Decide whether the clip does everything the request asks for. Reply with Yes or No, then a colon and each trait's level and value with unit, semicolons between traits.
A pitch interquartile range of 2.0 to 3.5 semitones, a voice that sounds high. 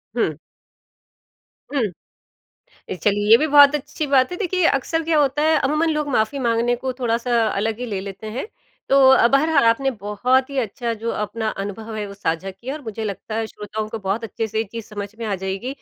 No: average, 4.6 semitones; high, 230 Hz